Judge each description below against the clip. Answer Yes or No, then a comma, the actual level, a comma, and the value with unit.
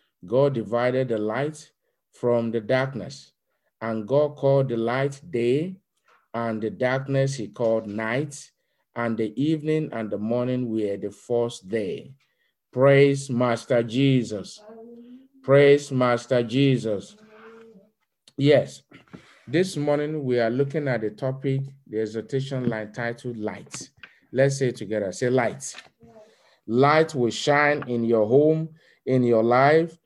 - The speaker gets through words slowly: Yes, slow, 130 wpm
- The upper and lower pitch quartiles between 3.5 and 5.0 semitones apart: Yes, average, 4.0 semitones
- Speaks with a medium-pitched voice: No, low, 130 Hz